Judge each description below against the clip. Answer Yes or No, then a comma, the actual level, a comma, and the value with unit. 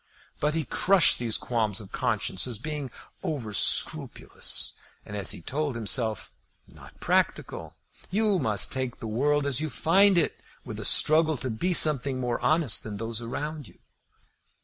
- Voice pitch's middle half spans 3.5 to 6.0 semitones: Yes, wide, 5.5 semitones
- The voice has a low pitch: Yes, low, 130 Hz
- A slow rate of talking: No, average, 160 wpm